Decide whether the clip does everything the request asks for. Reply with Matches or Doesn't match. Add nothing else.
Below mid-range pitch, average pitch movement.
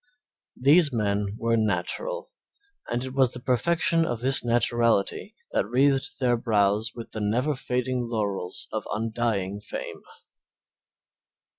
Matches